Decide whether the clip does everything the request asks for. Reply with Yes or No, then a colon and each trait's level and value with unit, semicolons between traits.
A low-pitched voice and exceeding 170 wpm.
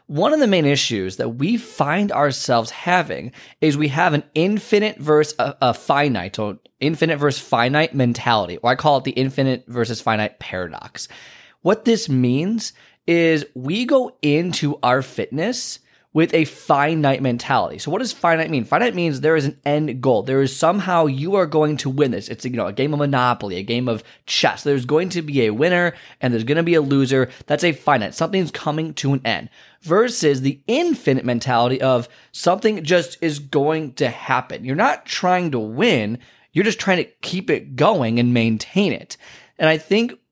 No: medium, 145 Hz; average, 190 wpm